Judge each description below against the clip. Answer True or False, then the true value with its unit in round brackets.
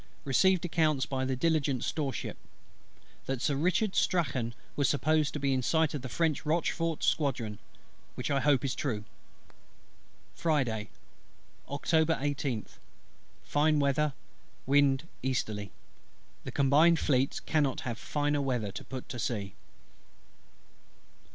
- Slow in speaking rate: True (120 wpm)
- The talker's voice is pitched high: False (140 Hz)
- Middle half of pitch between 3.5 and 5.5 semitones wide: False (3.1 semitones)